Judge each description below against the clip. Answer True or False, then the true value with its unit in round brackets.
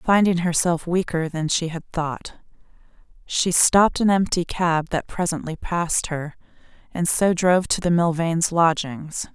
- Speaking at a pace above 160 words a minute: False (150 wpm)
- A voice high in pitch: False (170 Hz)